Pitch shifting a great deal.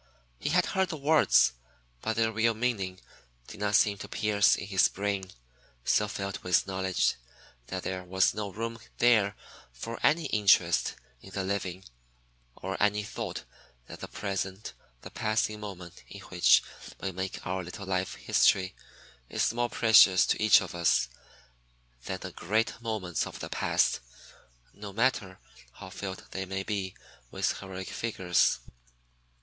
No: narrow, 2.5 semitones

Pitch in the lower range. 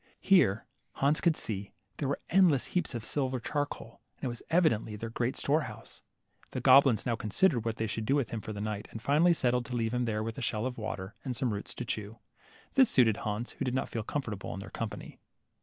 Yes: low, 120 Hz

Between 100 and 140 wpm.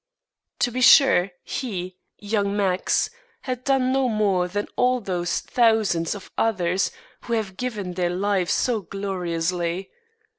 Yes: slow, 135 wpm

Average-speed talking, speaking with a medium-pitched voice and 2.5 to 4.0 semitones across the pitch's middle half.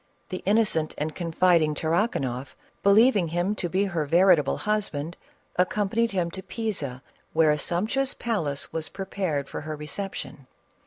No: average, 145 wpm; medium, 175 Hz; average, 4.8 semitones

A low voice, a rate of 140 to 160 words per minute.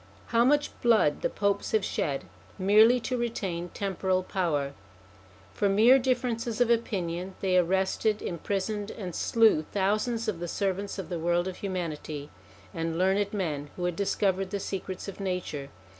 No: high, 195 Hz; average, 155 wpm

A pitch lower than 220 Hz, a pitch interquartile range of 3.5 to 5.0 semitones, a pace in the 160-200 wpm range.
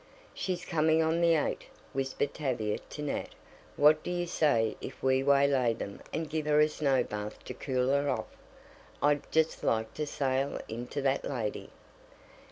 No: medium, 140 Hz; average, 3.0 semitones; average, 170 wpm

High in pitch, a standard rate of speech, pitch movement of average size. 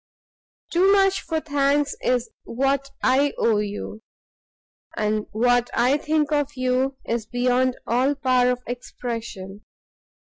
No: very high, 255 Hz; slow, 125 wpm; average, 3.3 semitones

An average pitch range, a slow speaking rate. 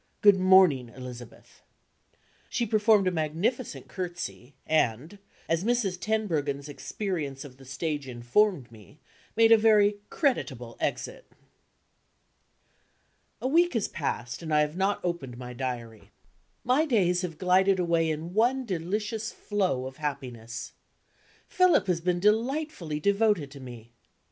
No: wide, 7.6 semitones; slow, 130 wpm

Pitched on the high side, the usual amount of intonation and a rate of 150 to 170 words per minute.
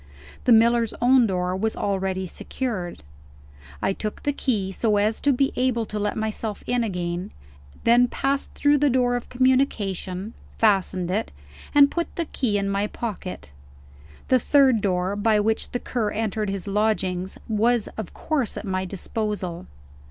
Yes: high, 215 Hz; average, 4.0 semitones; average, 160 wpm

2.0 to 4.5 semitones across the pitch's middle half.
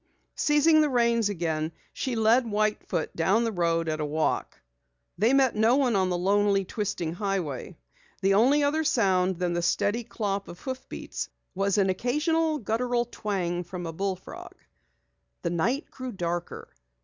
No: average, 5.3 semitones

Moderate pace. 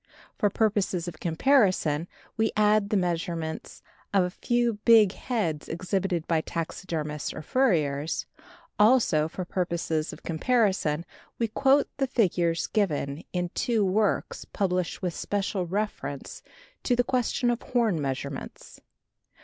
No: slow, 125 wpm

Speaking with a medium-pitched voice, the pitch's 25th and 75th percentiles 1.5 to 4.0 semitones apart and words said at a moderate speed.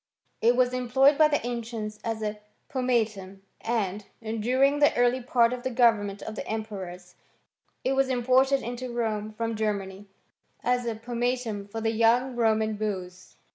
No: high, 230 Hz; average, 2.7 semitones; average, 155 wpm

